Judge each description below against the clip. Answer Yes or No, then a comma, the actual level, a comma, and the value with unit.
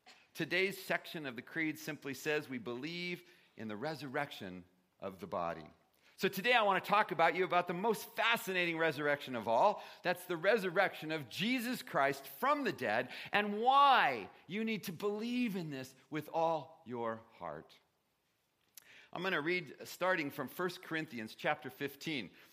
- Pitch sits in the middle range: Yes, medium, 165 Hz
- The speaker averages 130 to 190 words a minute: Yes, average, 165 wpm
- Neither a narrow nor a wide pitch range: No, wide, 5.8 semitones